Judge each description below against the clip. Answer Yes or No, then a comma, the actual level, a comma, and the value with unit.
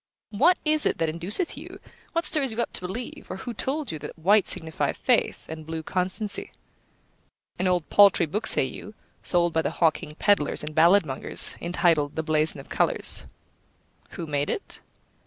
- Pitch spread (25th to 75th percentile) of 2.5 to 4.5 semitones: No, average, 5.0 semitones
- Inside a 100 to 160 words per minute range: No, average, 175 wpm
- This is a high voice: No, medium, 175 Hz